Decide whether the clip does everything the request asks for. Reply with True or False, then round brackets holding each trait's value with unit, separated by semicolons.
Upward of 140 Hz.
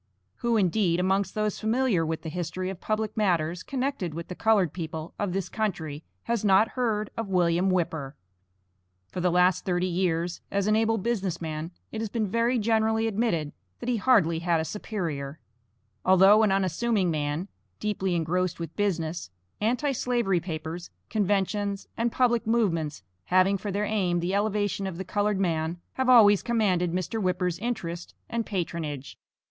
True (190 Hz)